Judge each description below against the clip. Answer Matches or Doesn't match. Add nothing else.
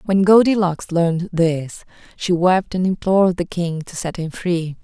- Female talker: Matches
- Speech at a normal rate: Matches